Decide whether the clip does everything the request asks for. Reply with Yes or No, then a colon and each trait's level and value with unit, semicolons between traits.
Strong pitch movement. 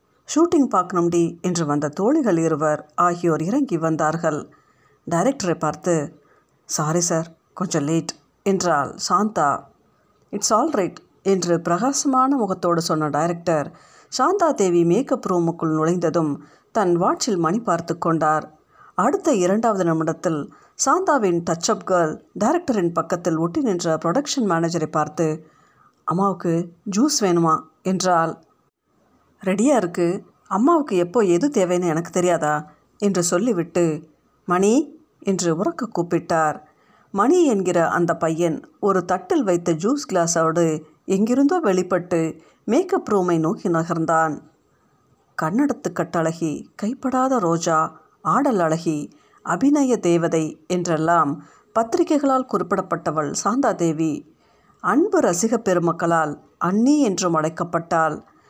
No: average, 4.4 semitones